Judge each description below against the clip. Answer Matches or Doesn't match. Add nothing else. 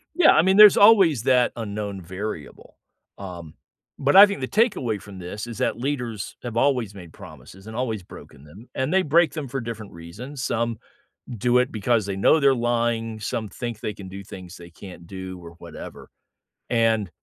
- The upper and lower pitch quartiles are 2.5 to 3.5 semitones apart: Doesn't match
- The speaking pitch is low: Matches